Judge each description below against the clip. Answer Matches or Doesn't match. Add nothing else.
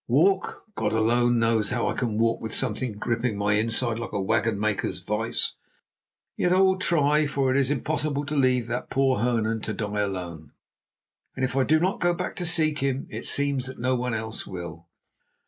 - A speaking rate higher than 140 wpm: Matches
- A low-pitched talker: Matches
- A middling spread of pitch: Matches